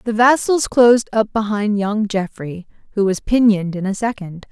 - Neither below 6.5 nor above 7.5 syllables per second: No, 4.9 syllables/s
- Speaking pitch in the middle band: No, high, 215 Hz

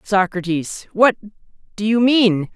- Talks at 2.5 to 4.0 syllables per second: Yes, 3.9 syllables/s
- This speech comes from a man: Yes, male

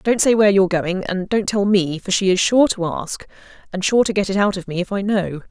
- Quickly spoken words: Yes, fast, 285 wpm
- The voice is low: No, high, 195 Hz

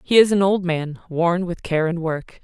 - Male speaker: No, female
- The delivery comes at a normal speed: No, fast, 245 wpm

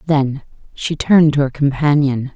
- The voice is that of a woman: Yes, female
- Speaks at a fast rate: No, average, 155 wpm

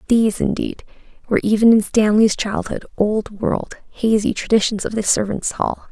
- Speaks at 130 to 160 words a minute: Yes, average, 150 wpm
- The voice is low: No, high, 215 Hz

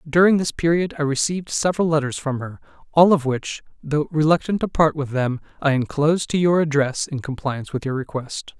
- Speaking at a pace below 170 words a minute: No, average, 195 wpm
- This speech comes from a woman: No, male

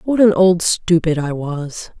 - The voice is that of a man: No, female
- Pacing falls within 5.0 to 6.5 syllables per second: No, 3.8 syllables/s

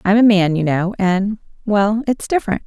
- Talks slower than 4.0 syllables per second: No, 4.9 syllables/s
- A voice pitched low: No, high, 200 Hz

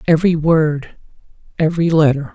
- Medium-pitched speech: Yes, medium, 160 Hz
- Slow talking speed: Yes, slow, 75 wpm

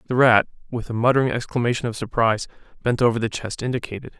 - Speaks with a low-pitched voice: Yes, low, 120 Hz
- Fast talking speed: No, average, 185 wpm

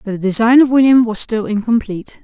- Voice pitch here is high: Yes, high, 225 Hz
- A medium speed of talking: No, fast, 215 wpm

